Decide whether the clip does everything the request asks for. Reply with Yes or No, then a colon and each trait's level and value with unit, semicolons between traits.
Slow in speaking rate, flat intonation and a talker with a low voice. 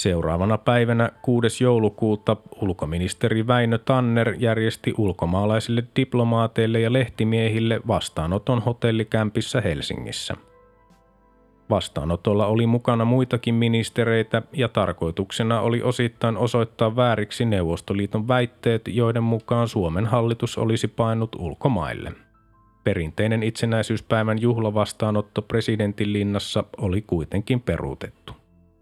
Yes: slow, 90 wpm; narrow, 2.1 semitones; low, 110 Hz